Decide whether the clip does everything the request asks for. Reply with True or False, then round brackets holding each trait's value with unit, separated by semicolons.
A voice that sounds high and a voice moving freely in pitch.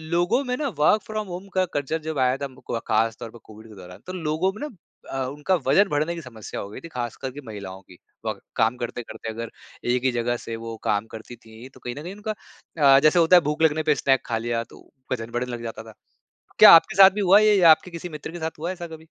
False (135 Hz; 6.9 semitones)